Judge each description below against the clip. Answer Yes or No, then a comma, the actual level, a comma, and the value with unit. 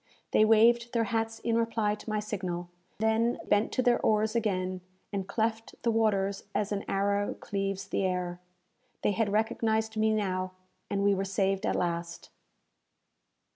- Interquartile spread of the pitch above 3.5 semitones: No, narrow, 2.4 semitones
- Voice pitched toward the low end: No, high, 210 Hz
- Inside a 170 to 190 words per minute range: No, average, 160 wpm